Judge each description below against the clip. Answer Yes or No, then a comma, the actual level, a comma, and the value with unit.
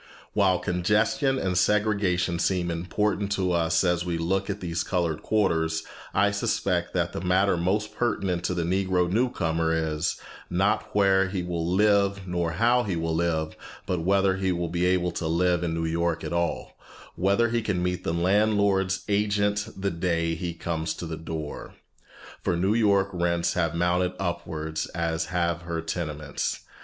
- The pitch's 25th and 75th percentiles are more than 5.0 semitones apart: No, average, 2.8 semitones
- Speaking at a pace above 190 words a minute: No, average, 170 wpm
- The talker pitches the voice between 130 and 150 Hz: No, very low, 90 Hz